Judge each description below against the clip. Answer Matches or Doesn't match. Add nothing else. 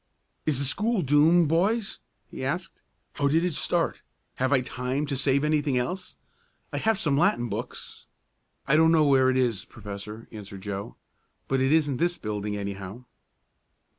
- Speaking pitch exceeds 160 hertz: Doesn't match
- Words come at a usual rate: Matches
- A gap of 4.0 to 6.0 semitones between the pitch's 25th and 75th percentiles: Matches